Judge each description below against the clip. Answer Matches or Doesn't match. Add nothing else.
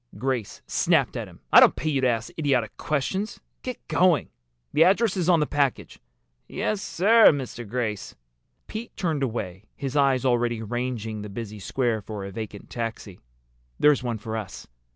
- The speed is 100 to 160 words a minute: Doesn't match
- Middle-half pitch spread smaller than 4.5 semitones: Doesn't match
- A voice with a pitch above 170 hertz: Doesn't match